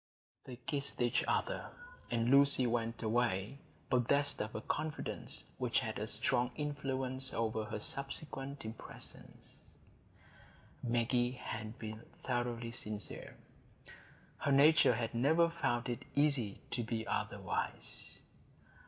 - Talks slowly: Yes, slow, 115 wpm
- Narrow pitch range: No, average, 3.3 semitones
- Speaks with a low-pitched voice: Yes, low, 120 Hz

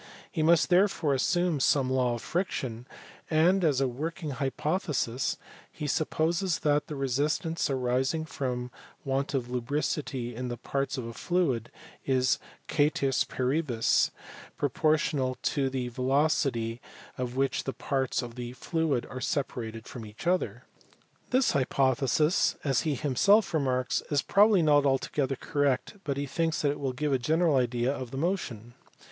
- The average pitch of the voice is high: No, low, 135 Hz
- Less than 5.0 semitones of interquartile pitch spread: Yes, average, 3.7 semitones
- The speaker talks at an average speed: Yes, average, 150 wpm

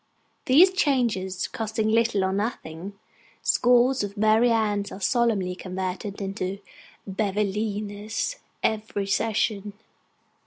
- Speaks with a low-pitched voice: No, high, 210 Hz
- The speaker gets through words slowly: Yes, slow, 95 wpm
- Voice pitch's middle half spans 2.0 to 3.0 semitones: Yes, narrow, 2.6 semitones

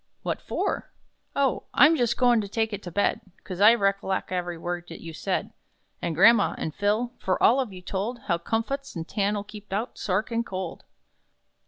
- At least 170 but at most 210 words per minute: Yes, average, 185 wpm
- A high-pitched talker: Yes, high, 205 Hz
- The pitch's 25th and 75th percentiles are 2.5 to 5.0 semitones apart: Yes, average, 4.0 semitones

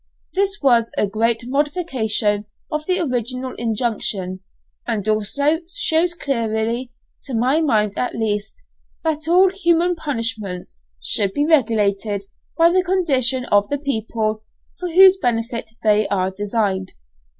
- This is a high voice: Yes, high, 235 Hz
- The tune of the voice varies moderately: No, wide, 6.6 semitones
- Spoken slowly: Yes, slow, 130 wpm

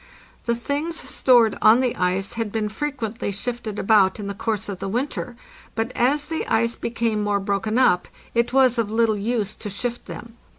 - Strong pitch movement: No, average, 2.9 semitones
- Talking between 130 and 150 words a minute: No, average, 185 wpm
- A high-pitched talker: Yes, high, 225 Hz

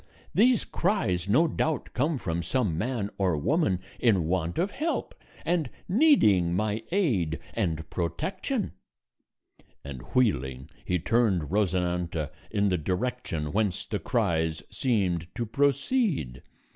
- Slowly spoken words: Yes, slow, 120 wpm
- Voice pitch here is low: Yes, low, 100 Hz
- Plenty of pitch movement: Yes, wide, 8.3 semitones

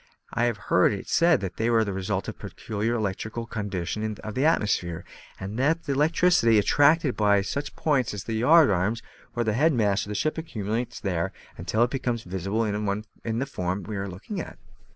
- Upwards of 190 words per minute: Yes, fast, 205 wpm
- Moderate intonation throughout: Yes, average, 4.5 semitones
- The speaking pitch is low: Yes, low, 110 Hz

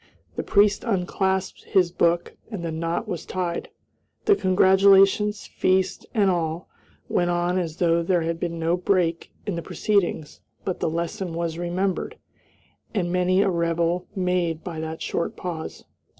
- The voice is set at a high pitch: No, medium, 175 Hz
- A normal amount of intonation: No, narrow, 2.1 semitones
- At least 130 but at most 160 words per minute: Yes, average, 150 wpm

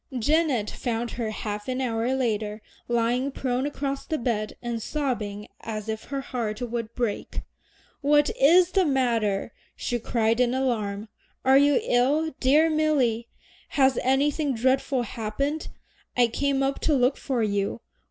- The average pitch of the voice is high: Yes, very high, 250 Hz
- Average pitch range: Yes, average, 3.6 semitones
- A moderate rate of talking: Yes, average, 145 wpm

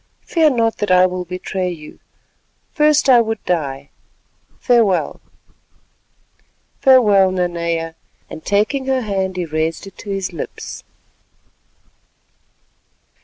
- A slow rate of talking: Yes, slow, 105 wpm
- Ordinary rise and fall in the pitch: Yes, average, 4.8 semitones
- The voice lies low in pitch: No, high, 190 Hz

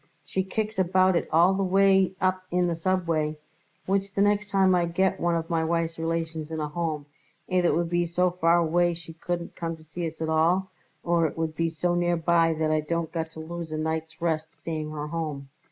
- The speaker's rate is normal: No, fast, 220 wpm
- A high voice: No, medium, 170 Hz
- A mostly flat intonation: Yes, narrow, 2.1 semitones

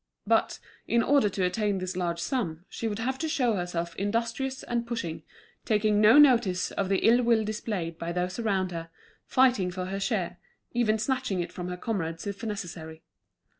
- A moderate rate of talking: Yes, average, 180 wpm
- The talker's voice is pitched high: Yes, high, 205 Hz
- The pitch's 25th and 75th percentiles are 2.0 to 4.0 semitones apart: No, average, 4.6 semitones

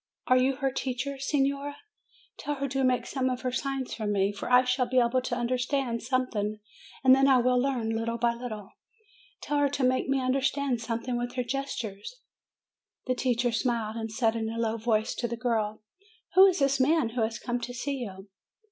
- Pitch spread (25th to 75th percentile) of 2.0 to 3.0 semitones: Yes, narrow, 2.6 semitones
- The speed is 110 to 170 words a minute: No, average, 200 wpm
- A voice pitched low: No, very high, 250 Hz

